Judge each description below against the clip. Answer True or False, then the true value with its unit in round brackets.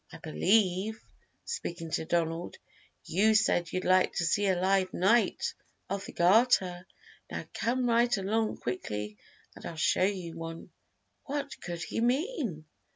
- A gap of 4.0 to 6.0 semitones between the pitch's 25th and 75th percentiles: True (4.9 semitones)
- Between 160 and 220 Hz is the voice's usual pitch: True (185 Hz)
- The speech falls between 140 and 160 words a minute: True (145 wpm)